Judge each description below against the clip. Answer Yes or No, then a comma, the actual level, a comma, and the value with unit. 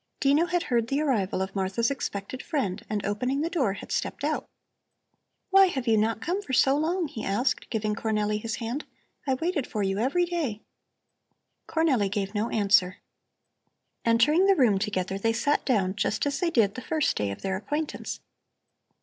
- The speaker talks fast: No, average, 180 wpm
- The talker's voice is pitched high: Yes, high, 230 Hz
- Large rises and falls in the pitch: Yes, wide, 6.3 semitones